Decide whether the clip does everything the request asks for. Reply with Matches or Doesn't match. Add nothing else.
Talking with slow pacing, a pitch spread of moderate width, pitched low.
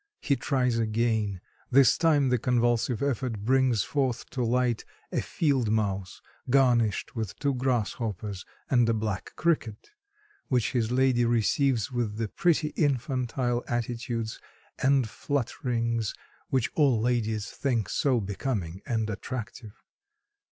Matches